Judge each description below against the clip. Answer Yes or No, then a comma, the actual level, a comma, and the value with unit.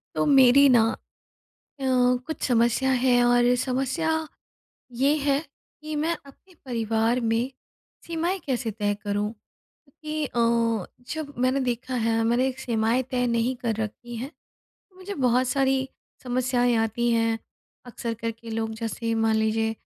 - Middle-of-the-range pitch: No, high, 245 Hz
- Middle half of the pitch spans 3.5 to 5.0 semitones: No, average, 3.0 semitones